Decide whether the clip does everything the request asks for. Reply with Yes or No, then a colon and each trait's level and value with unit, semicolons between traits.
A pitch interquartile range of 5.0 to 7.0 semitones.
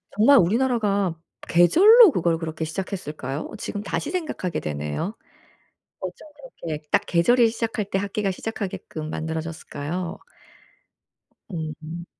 Yes: wide, 5.5 semitones